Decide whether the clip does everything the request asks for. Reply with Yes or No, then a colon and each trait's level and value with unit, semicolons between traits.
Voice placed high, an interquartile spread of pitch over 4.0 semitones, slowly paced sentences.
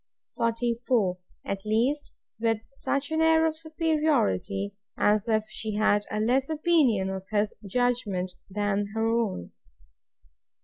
Yes: high, 225 Hz; average, 5.0 semitones; slow, 125 wpm